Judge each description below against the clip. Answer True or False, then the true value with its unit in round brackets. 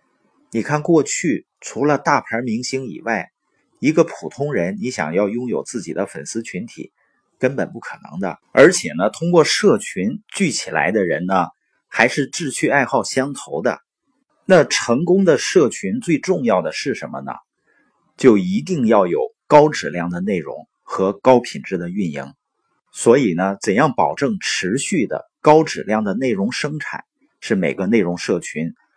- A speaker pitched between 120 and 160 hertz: True (140 Hz)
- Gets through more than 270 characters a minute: False (235 characters per minute)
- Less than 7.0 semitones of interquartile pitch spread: False (7.5 semitones)